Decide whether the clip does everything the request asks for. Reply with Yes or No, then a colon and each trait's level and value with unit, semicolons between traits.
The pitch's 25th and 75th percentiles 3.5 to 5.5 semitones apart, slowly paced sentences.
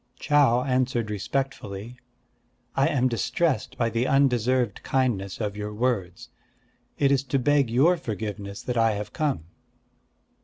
Yes: average, 4.3 semitones; slow, 130 wpm